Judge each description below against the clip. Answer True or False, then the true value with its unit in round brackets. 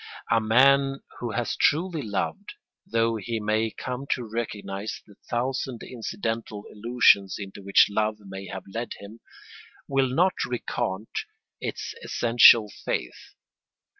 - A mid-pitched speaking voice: False (115 Hz)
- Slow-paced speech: True (125 wpm)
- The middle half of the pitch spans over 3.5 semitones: False (3.2 semitones)